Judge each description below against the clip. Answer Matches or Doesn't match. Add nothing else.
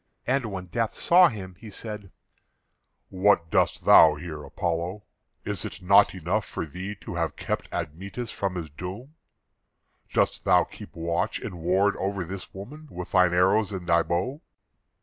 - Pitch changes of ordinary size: Matches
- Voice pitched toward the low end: Matches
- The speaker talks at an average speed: Matches